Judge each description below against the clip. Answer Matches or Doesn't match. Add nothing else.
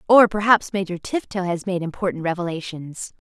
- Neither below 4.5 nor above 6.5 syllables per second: Matches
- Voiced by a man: Doesn't match